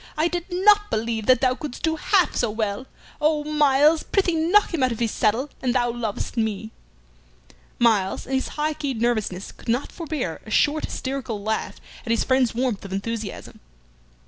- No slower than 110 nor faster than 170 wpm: No, average, 180 wpm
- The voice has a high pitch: Yes, very high, 255 Hz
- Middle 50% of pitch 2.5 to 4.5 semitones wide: No, wide, 5.5 semitones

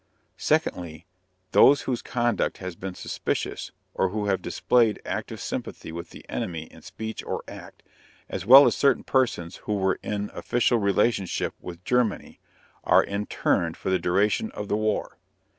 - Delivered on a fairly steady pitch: No, average, 4.5 semitones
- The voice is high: No, low, 100 Hz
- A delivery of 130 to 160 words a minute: Yes, average, 155 wpm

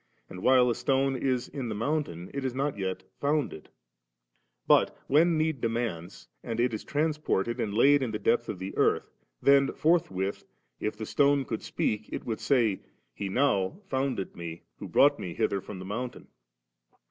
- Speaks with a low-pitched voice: Yes, low, 120 Hz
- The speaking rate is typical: Yes, average, 175 wpm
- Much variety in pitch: Yes, wide, 5.8 semitones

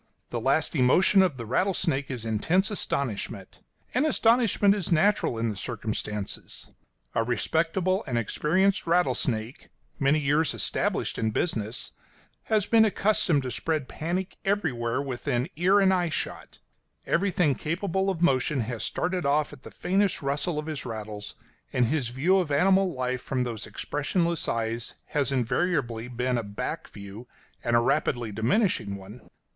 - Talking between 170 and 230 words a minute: No, average, 150 wpm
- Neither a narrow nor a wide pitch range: No, wide, 7.2 semitones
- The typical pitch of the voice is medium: Yes, medium, 145 Hz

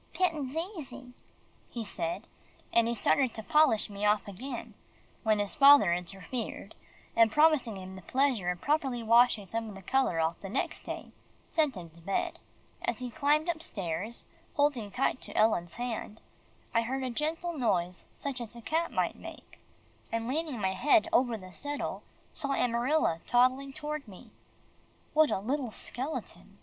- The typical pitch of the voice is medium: No, high, 240 Hz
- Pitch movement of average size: No, wide, 5.7 semitones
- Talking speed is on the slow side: No, average, 165 wpm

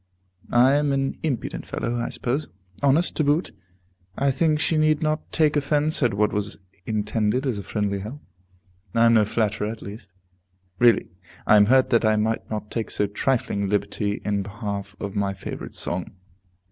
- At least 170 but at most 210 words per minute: Yes, average, 180 wpm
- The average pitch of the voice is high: No, low, 115 Hz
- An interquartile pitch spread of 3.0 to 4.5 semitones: No, average, 5.2 semitones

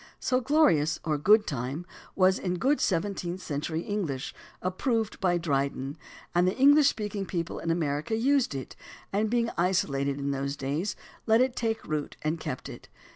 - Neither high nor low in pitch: Yes, medium, 180 Hz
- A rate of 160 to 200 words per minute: Yes, average, 170 wpm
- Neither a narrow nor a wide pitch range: No, wide, 7.0 semitones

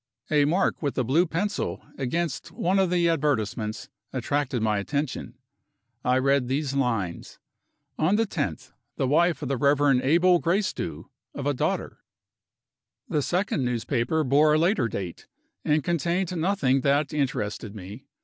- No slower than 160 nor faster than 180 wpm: No, average, 150 wpm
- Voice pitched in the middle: Yes, medium, 145 Hz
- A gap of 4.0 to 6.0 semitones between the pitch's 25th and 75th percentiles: Yes, average, 5.0 semitones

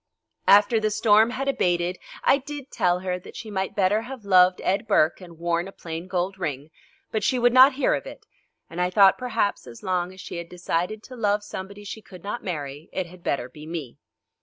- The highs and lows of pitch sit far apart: No, average, 3.7 semitones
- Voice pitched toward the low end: No, medium, 185 Hz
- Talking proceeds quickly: Yes, fast, 215 wpm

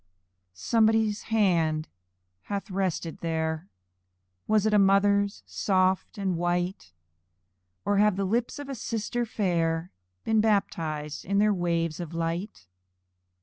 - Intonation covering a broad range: No, average, 4.0 semitones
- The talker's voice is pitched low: No, high, 190 Hz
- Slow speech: Yes, slow, 120 wpm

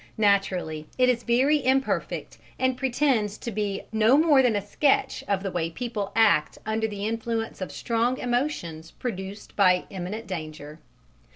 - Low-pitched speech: No, high, 220 Hz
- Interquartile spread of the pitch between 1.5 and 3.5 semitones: No, average, 4.5 semitones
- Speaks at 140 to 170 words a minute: Yes, average, 155 wpm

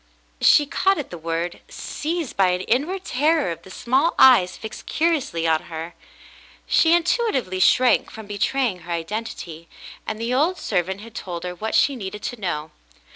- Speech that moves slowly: No, average, 170 wpm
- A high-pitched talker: Yes, high, 215 Hz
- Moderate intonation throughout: No, wide, 8.2 semitones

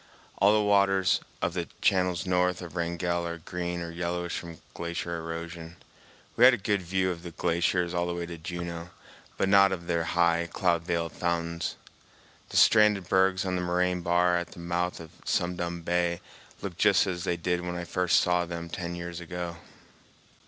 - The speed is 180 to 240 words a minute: Yes, average, 190 wpm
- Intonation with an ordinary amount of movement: No, narrow, 1.1 semitones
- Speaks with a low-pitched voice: Yes, very low, 85 Hz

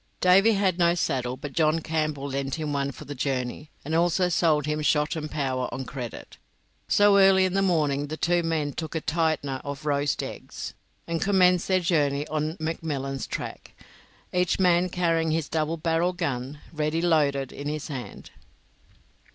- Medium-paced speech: Yes, average, 170 wpm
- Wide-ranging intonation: No, average, 3.3 semitones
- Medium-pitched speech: Yes, medium, 155 Hz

